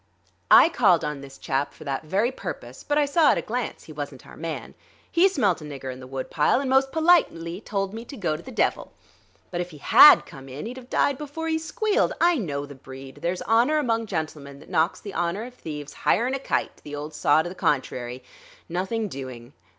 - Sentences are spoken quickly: Yes, fast, 220 wpm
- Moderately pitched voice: Yes, medium, 175 Hz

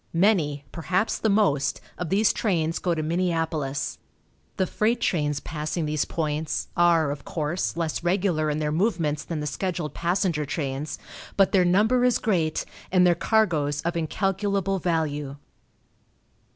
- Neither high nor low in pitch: Yes, medium, 165 Hz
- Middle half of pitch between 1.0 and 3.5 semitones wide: No, average, 3.9 semitones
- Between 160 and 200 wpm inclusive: No, average, 145 wpm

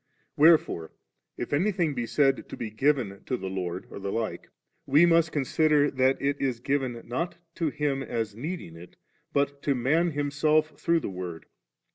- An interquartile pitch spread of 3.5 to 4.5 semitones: No, average, 4.9 semitones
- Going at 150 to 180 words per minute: Yes, average, 170 wpm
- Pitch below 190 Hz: Yes, medium, 140 Hz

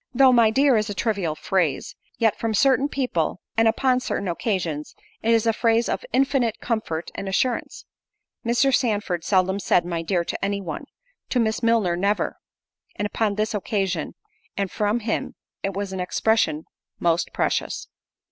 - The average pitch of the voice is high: Yes, high, 210 Hz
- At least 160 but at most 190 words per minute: Yes, average, 165 wpm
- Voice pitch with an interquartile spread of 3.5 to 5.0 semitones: Yes, average, 4.0 semitones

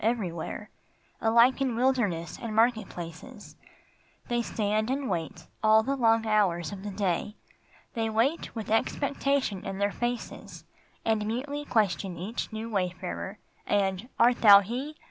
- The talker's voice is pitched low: No, high, 220 Hz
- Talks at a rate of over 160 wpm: No, average, 145 wpm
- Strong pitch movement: No, average, 3.4 semitones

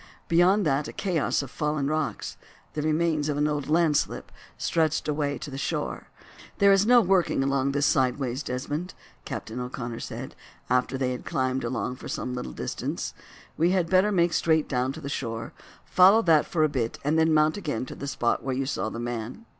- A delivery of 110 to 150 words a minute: No, average, 195 wpm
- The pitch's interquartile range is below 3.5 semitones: No, average, 4.1 semitones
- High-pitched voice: No, medium, 145 Hz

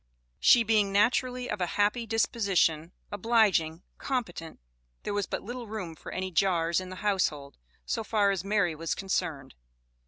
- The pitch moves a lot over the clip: No, average, 4.5 semitones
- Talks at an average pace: Yes, average, 155 wpm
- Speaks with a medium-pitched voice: No, high, 200 Hz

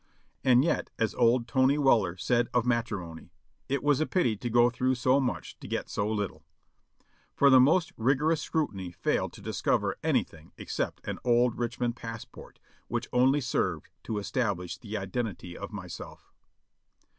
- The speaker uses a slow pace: No, average, 160 wpm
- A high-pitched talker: No, low, 120 Hz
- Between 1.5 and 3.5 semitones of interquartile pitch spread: No, average, 4.0 semitones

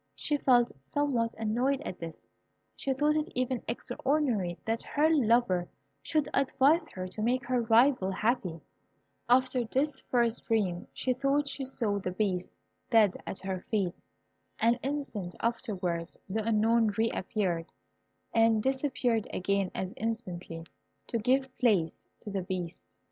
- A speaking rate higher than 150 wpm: No, average, 140 wpm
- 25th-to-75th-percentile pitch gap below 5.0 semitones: No, average, 5.3 semitones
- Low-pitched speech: No, high, 230 Hz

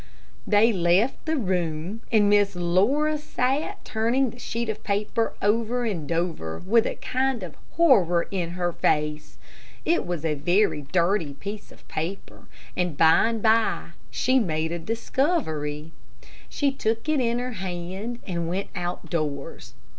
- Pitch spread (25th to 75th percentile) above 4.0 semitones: Yes, wide, 5.6 semitones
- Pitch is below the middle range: No, high, 200 Hz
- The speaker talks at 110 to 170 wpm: Yes, average, 150 wpm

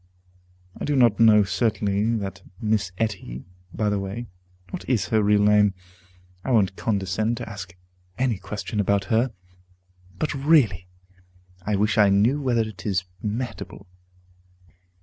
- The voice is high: No, low, 105 Hz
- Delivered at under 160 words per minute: Yes, average, 140 wpm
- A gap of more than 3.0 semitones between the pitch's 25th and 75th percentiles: No, average, 2.7 semitones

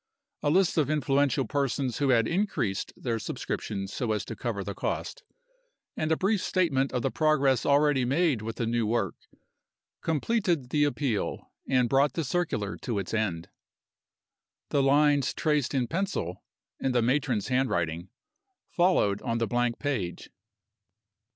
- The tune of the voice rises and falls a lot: No, average, 4.7 semitones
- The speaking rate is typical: Yes, average, 150 wpm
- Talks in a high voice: No, low, 130 Hz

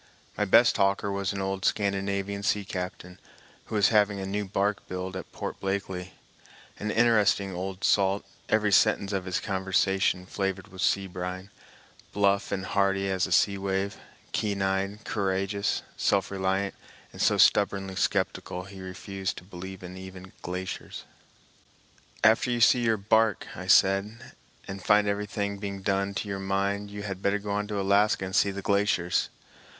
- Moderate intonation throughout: No, narrow, 1.2 semitones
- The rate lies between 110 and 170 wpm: Yes, average, 160 wpm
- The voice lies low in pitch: Yes, low, 100 Hz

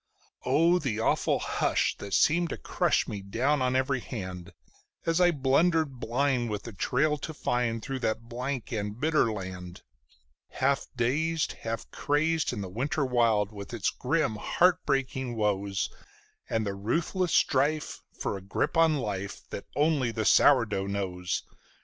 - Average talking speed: Yes, average, 155 wpm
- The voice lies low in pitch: Yes, low, 125 Hz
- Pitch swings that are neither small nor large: No, wide, 6.1 semitones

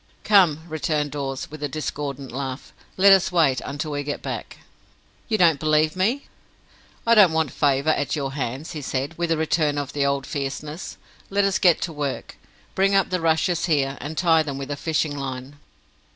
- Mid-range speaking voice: Yes, medium, 150 Hz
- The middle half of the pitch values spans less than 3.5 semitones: Yes, average, 3.1 semitones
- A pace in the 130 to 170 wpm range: No, average, 190 wpm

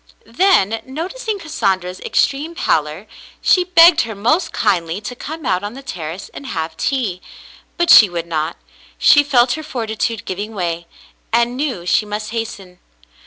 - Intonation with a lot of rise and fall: Yes, wide, 7.9 semitones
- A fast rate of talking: No, average, 155 wpm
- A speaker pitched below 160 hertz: No, high, 225 Hz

